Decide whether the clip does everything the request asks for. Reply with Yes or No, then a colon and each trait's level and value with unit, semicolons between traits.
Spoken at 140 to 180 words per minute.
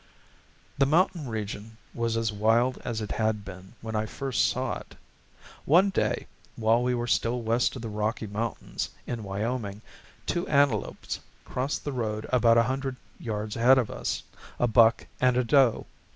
Yes: average, 165 wpm